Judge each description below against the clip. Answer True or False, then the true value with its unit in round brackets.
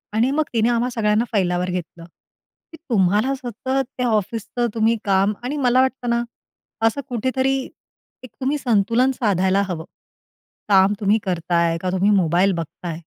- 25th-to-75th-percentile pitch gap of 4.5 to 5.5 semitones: True (4.8 semitones)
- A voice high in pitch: True (215 Hz)